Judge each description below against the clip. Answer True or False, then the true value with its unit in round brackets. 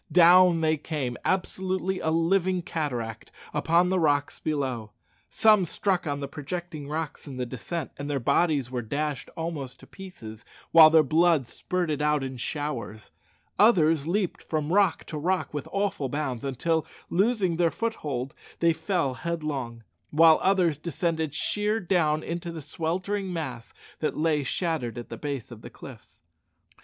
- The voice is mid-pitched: True (160 Hz)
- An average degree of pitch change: True (3.8 semitones)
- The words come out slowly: False (155 wpm)